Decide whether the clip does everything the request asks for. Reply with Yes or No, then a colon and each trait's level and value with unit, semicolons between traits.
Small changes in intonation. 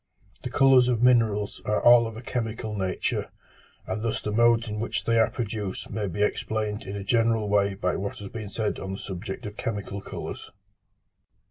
Yes: narrow, 2.2 semitones